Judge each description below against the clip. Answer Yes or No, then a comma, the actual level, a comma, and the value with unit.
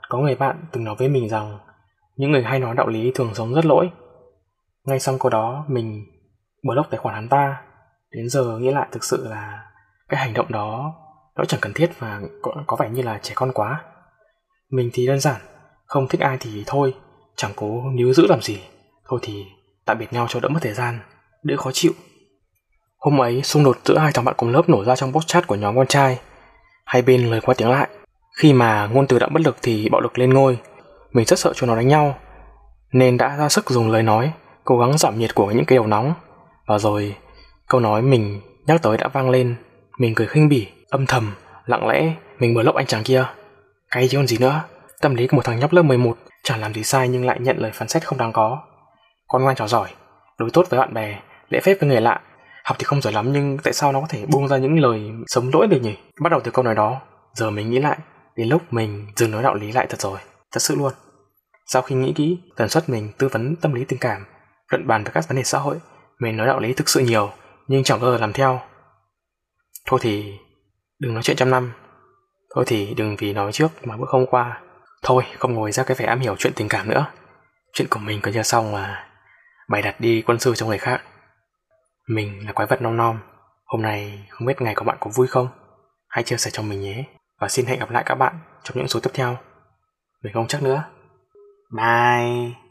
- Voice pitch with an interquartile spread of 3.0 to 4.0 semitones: Yes, average, 3.5 semitones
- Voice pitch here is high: No, low, 125 Hz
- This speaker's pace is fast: No, average, 235 wpm